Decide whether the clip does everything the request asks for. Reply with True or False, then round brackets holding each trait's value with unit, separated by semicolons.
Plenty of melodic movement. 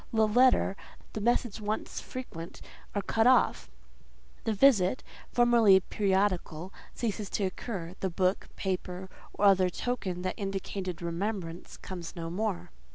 False (3.3 semitones)